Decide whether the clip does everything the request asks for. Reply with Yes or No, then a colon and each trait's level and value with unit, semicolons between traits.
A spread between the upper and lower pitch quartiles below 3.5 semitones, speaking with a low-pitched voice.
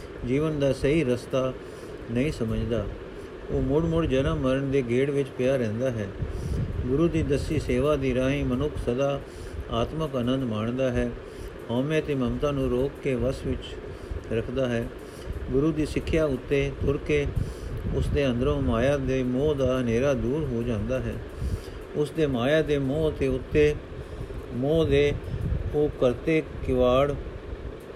Yes: average, 2.9 semitones; low, 130 Hz